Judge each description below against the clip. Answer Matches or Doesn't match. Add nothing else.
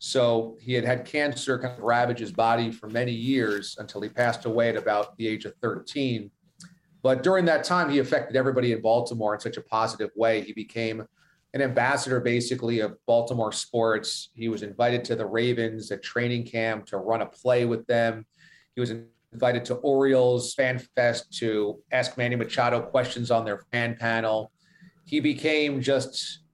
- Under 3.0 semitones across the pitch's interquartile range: Matches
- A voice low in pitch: Matches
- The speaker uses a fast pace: Doesn't match